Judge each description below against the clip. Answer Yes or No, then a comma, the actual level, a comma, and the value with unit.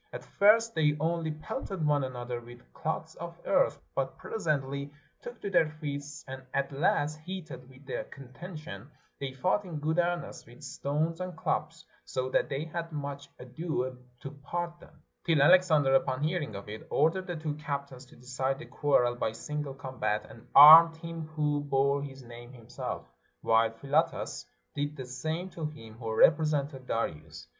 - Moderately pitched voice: Yes, medium, 145 Hz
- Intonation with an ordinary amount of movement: Yes, average, 3.8 semitones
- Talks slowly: No, average, 165 wpm